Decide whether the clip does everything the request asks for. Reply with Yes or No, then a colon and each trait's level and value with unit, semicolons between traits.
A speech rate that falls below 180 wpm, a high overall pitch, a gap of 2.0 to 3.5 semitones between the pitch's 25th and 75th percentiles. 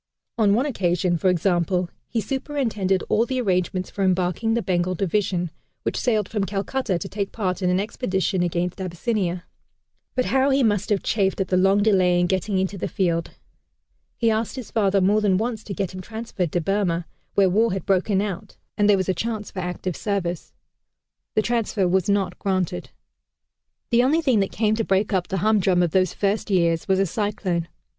No: average, 195 wpm; high, 195 Hz; average, 2.9 semitones